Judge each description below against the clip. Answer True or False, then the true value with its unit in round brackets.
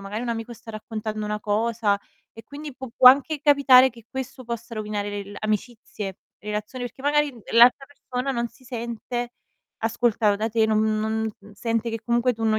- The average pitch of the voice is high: True (230 Hz)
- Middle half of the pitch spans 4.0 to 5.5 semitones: False (2.6 semitones)